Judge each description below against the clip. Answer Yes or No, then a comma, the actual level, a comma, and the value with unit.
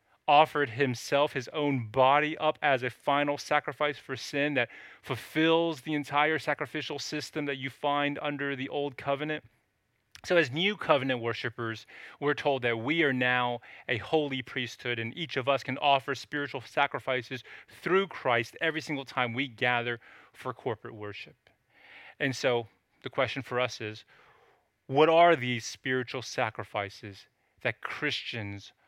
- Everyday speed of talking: Yes, average, 150 wpm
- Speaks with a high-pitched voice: No, low, 135 Hz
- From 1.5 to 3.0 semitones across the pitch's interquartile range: No, average, 3.5 semitones